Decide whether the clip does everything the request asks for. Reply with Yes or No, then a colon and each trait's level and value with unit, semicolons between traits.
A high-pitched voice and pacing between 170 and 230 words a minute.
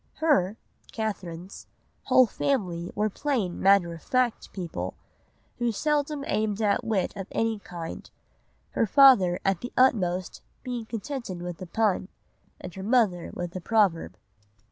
No: high, 205 Hz; average, 140 wpm